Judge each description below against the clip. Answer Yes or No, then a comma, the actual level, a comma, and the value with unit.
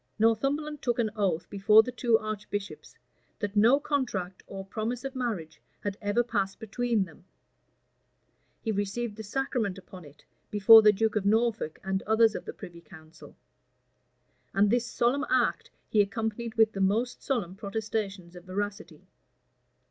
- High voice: Yes, high, 215 Hz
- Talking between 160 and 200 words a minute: No, average, 150 wpm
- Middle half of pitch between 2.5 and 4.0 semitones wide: Yes, average, 3.3 semitones